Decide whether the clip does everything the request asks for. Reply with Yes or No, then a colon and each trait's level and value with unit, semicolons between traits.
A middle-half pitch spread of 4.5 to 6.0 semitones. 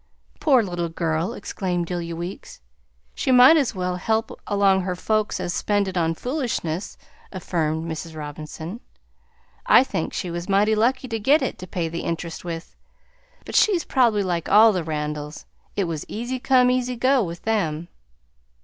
Yes: wide, 5.4 semitones